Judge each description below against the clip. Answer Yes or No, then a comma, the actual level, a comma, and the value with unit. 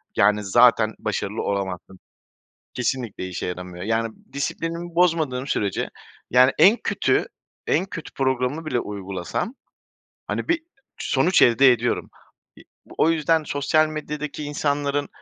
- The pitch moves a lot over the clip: Yes, wide, 6.6 semitones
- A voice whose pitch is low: Yes, low, 130 Hz